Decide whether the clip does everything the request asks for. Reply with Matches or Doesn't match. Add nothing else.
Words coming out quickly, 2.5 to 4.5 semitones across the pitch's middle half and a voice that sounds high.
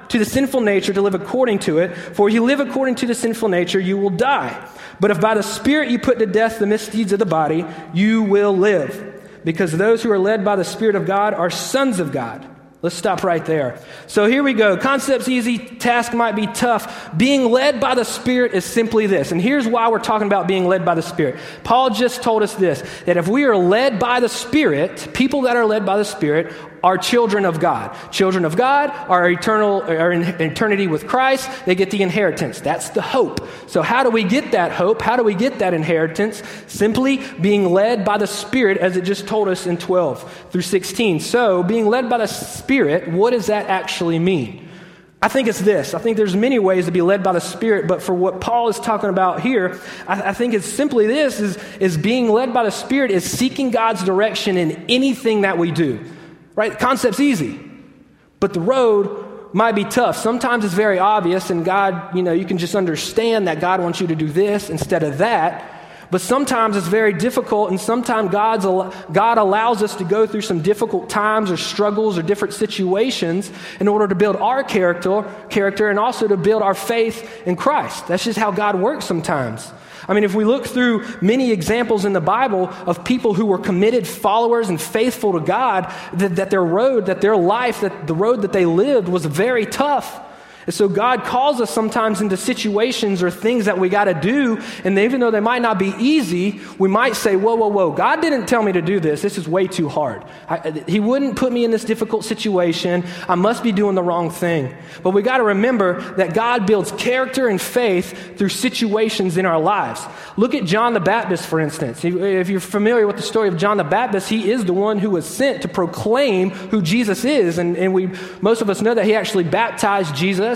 Matches